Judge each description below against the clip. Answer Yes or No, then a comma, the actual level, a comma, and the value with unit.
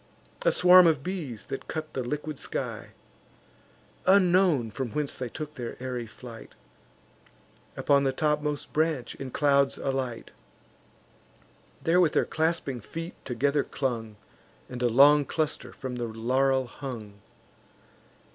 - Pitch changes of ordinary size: Yes, average, 3.8 semitones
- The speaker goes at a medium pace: No, slow, 130 wpm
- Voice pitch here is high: No, low, 135 Hz